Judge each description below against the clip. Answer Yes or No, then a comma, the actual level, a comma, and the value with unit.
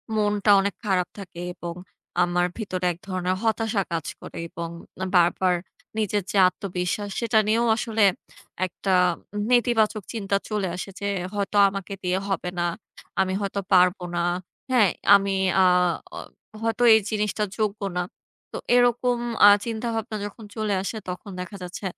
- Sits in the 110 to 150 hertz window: No, high, 200 Hz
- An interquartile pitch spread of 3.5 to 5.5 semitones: No, average, 3.1 semitones